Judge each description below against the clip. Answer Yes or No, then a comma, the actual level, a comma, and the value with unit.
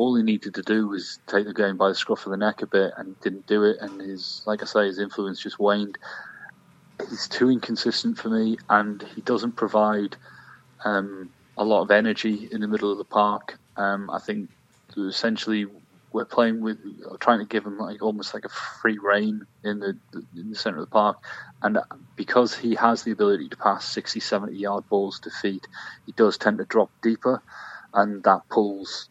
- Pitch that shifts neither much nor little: No, narrow, 1.8 semitones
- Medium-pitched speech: No, low, 105 Hz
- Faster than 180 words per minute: Yes, average, 200 wpm